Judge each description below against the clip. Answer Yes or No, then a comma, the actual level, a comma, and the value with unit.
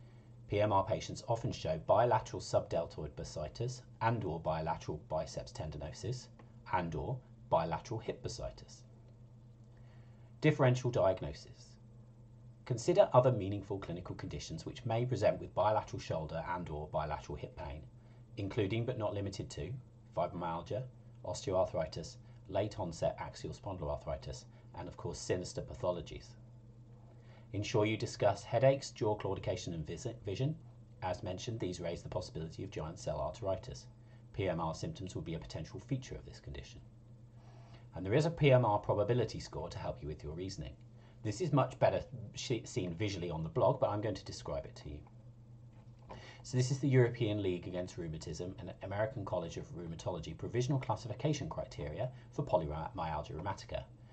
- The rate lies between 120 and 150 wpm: Yes, average, 140 wpm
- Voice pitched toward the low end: Yes, low, 120 Hz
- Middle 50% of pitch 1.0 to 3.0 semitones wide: Yes, narrow, 2.6 semitones